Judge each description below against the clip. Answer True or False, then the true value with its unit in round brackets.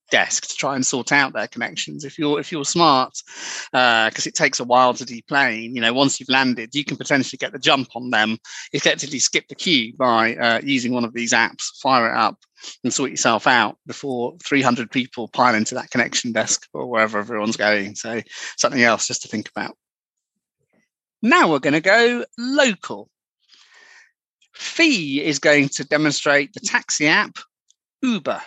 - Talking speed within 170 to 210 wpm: True (185 wpm)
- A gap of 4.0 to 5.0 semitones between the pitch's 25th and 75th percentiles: True (4.5 semitones)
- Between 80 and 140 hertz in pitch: True (135 Hz)